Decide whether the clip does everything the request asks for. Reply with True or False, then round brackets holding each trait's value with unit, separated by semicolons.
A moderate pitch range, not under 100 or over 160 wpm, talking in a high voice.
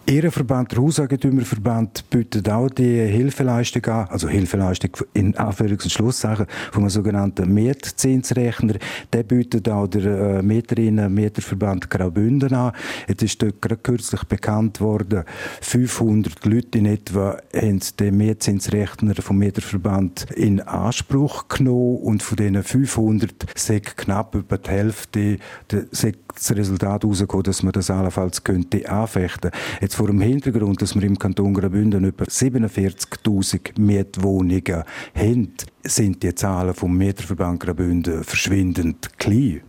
False (3.0 semitones; 125 wpm; 105 Hz)